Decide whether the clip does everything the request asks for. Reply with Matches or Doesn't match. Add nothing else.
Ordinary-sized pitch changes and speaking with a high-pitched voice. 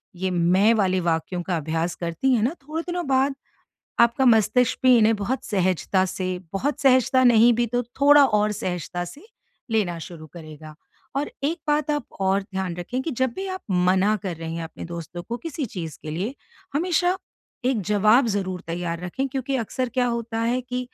Doesn't match